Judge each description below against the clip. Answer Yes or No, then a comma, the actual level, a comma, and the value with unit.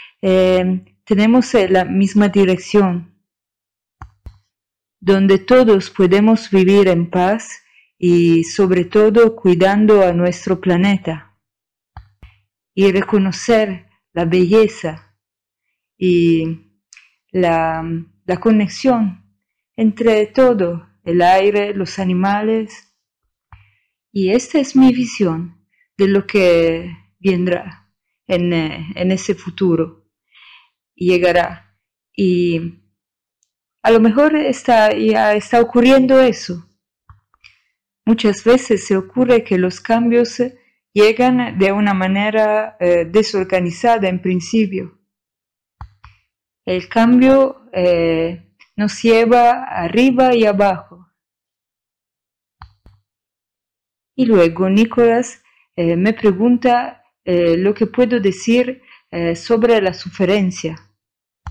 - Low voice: No, medium, 185 Hz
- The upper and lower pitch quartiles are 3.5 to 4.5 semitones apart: No, average, 5.2 semitones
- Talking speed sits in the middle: No, slow, 90 wpm